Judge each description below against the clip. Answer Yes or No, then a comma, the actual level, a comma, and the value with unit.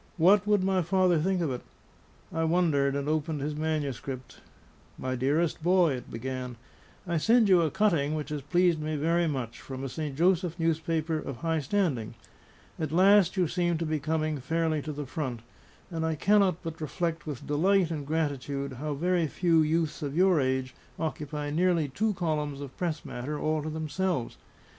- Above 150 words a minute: Yes, average, 180 wpm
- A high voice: No, medium, 155 Hz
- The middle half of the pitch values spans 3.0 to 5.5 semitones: Yes, average, 3.3 semitones